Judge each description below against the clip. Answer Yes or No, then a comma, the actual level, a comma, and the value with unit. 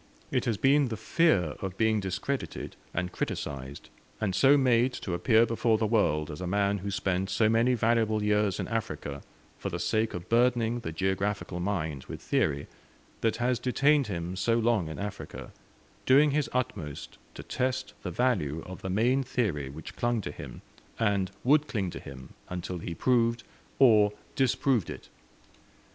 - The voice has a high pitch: No, low, 105 Hz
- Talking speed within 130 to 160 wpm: No, average, 170 wpm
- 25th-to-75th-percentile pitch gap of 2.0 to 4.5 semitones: No, average, 5.0 semitones